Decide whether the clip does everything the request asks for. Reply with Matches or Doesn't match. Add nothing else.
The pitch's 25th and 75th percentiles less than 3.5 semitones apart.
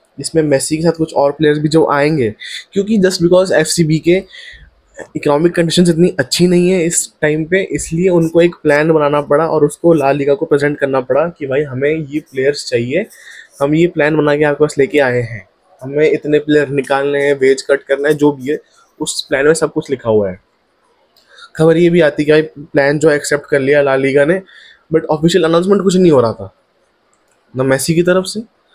Matches